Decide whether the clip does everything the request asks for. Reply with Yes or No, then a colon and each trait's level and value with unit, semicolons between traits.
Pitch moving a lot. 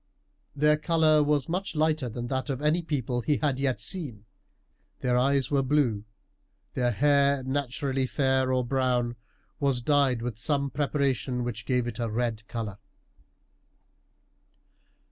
No: average, 3.0 semitones